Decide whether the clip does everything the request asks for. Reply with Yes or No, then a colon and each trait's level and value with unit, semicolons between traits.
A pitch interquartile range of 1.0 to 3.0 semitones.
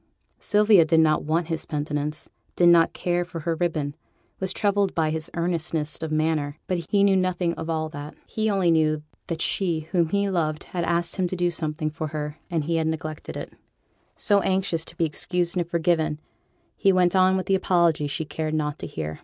Yes: narrow, 2.6 semitones